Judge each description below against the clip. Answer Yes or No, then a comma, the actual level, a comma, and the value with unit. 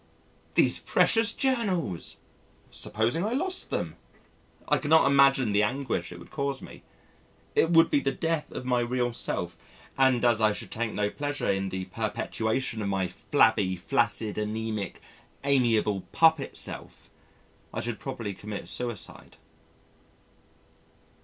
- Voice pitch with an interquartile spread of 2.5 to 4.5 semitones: No, average, 5.0 semitones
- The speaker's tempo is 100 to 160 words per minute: Yes, slow, 135 wpm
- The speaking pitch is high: No, low, 120 Hz